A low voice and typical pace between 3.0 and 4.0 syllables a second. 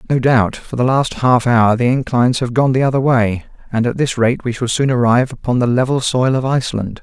No: low, 125 Hz; 5.6 syllables/s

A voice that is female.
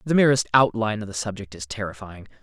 No: male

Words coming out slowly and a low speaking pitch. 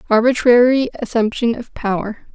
No: slow, 100 wpm; high, 230 Hz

